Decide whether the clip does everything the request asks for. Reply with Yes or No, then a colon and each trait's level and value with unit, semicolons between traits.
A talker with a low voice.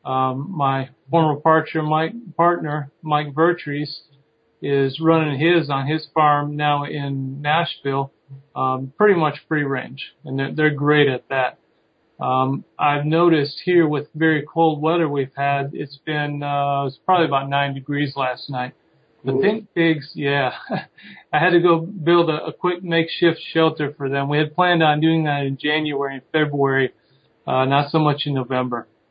No: medium, 150 Hz